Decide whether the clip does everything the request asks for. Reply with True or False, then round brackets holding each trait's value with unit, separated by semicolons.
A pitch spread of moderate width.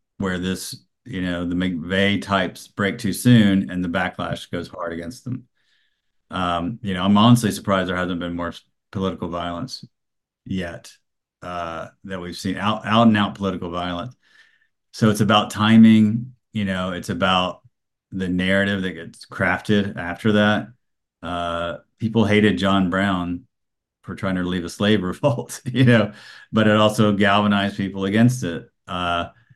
True (3.1 semitones)